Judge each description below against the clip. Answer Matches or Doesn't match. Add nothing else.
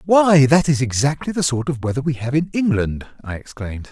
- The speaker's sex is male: Matches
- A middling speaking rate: Doesn't match